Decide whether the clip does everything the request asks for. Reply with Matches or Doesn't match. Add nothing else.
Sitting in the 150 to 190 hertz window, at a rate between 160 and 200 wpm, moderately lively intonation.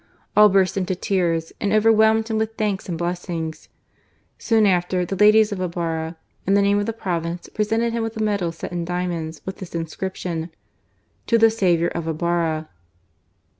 Matches